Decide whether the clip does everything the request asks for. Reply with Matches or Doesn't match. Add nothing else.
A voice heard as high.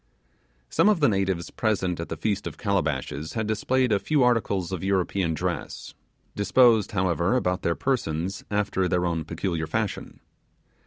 Doesn't match